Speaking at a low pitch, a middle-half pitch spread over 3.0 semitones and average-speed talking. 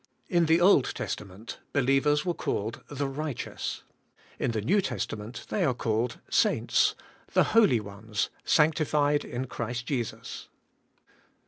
No: low, 130 Hz; average, 5.2 semitones; slow, 130 wpm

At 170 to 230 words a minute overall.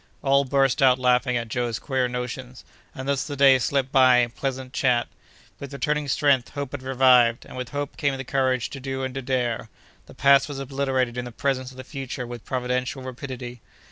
Yes: fast, 205 wpm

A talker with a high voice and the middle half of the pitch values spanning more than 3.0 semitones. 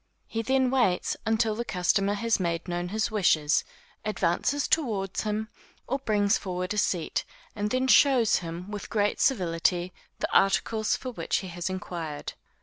Yes: high, 205 Hz; average, 4.0 semitones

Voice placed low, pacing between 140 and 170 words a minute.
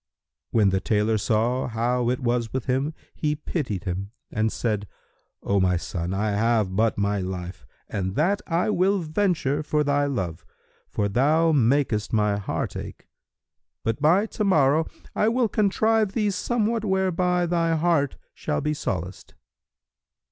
Yes: low, 130 Hz; average, 150 wpm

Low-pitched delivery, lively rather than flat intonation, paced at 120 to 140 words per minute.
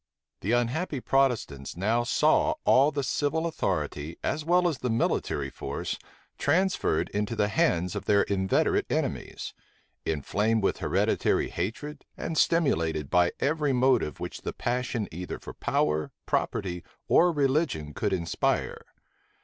Yes: low, 115 Hz; wide, 8.6 semitones; slow, 135 wpm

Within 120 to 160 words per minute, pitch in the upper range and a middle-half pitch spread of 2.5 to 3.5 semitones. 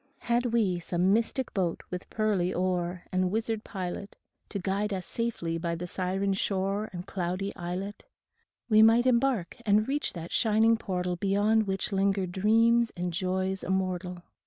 Yes: average, 155 wpm; high, 195 Hz; average, 3.2 semitones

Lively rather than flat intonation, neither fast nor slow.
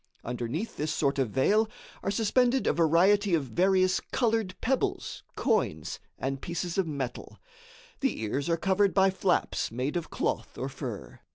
Yes: wide, 6.6 semitones; average, 155 wpm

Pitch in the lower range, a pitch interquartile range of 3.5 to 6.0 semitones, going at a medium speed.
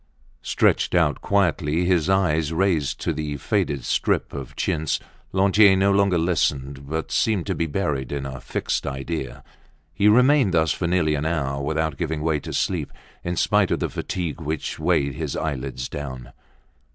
Yes: very low, 80 Hz; average, 4.1 semitones; average, 165 wpm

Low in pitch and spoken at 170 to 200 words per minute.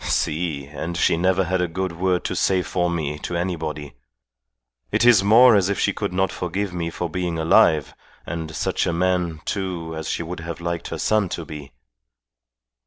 Yes: very low, 85 Hz; average, 190 wpm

